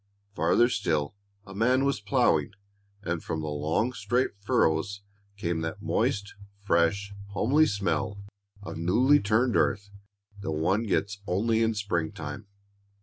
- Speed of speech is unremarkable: No, slow, 130 wpm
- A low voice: Yes, low, 100 Hz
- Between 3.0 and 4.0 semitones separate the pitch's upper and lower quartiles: No, average, 5.0 semitones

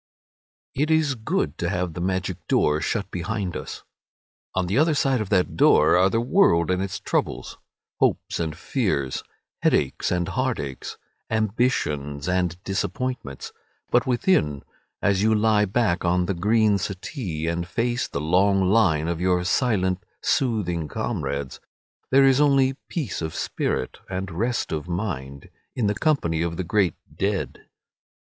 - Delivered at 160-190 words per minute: No, average, 150 wpm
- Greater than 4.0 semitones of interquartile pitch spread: Yes, average, 5.2 semitones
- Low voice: Yes, very low, 95 Hz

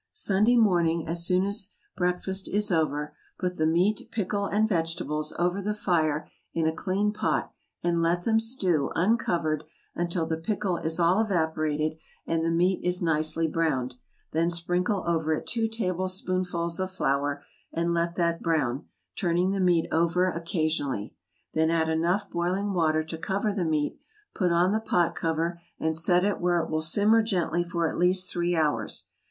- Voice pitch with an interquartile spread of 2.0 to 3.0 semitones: Yes, average, 2.7 semitones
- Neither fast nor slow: Yes, average, 170 wpm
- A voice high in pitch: No, medium, 170 Hz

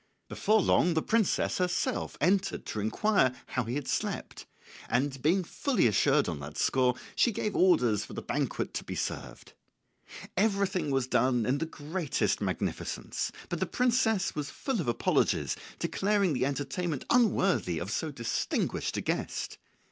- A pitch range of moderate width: No, wide, 7.5 semitones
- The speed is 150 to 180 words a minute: Yes, average, 155 wpm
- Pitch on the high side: No, medium, 160 Hz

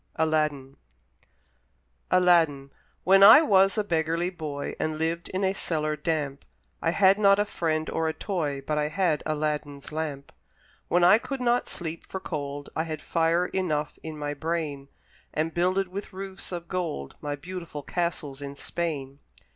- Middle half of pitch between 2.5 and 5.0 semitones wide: Yes, average, 3.6 semitones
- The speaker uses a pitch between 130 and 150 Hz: No, medium, 160 Hz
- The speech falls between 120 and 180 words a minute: Yes, average, 160 wpm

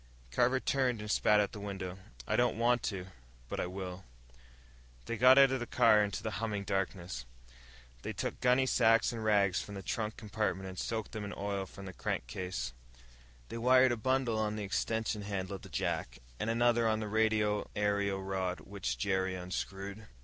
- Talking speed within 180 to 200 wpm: Yes, average, 185 wpm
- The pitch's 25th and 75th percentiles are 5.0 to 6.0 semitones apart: No, average, 3.0 semitones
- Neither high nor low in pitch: No, low, 105 Hz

